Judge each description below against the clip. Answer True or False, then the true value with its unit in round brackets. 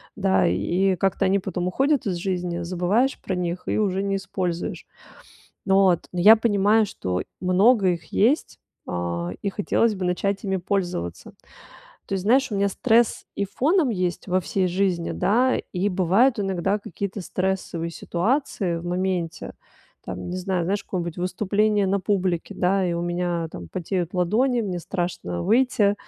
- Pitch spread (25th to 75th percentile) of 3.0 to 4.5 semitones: False (2.6 semitones)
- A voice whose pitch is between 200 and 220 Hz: False (190 Hz)